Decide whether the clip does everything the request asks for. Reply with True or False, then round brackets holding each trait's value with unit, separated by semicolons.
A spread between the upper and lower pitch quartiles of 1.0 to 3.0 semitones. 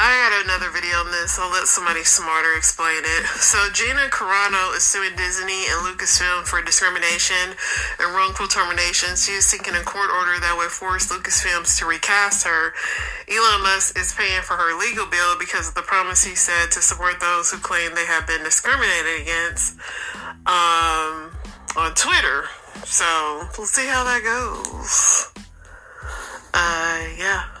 True (2.7 semitones)